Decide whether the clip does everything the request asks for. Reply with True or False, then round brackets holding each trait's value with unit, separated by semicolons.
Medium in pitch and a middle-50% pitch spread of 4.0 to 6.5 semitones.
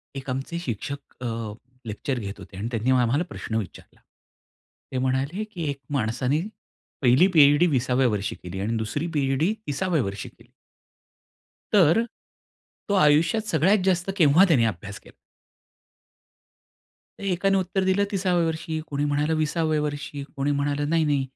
True (145 Hz; 4.8 semitones)